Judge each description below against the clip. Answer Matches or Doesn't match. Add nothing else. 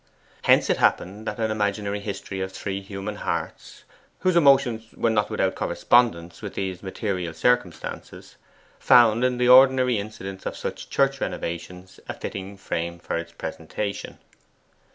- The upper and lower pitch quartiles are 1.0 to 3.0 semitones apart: Doesn't match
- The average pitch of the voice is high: Doesn't match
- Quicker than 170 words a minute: Doesn't match